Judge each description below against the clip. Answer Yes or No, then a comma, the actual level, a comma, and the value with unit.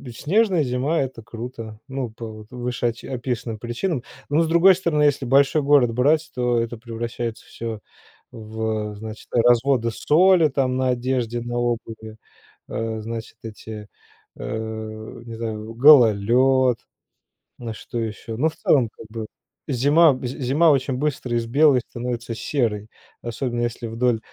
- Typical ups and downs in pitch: Yes, average, 3.2 semitones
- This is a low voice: Yes, low, 120 Hz